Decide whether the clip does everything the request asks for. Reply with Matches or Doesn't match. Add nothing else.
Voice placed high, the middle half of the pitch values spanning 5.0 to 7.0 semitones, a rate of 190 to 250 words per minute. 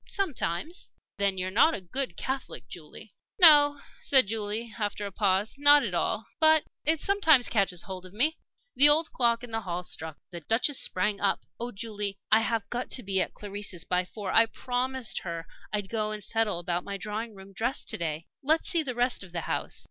Matches